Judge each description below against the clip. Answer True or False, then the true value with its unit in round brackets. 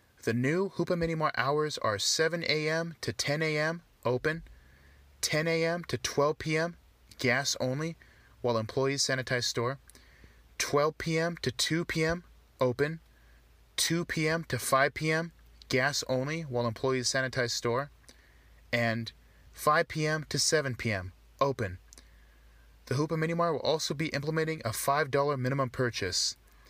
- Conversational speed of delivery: False (130 wpm)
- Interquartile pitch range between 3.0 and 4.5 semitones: False (5.0 semitones)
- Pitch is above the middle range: False (140 Hz)